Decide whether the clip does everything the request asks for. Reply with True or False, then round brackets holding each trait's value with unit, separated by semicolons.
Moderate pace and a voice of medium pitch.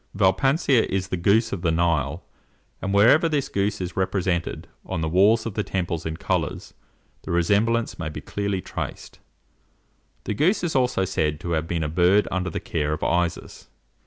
False (180 wpm; 95 Hz)